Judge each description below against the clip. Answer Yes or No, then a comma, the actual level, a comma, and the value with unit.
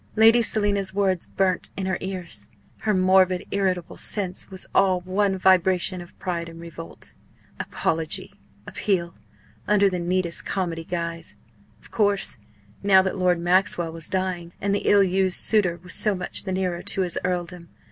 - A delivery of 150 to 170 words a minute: Yes, average, 155 wpm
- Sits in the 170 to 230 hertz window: Yes, medium, 185 Hz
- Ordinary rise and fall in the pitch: No, narrow, 1.9 semitones